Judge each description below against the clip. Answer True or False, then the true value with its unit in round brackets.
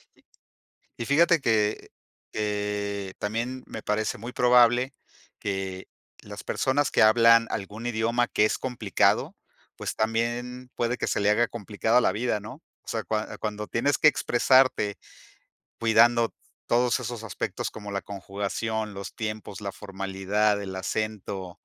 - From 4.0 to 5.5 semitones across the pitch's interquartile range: False (2.8 semitones)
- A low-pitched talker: True (110 Hz)